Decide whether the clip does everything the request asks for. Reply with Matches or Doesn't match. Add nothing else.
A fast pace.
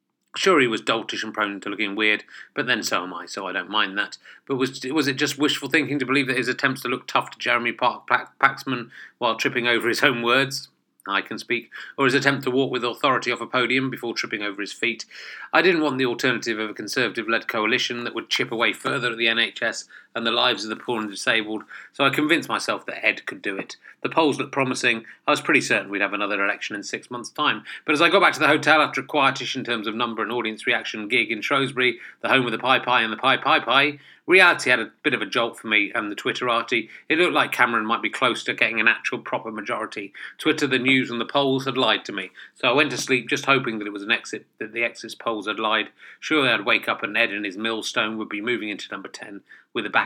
Matches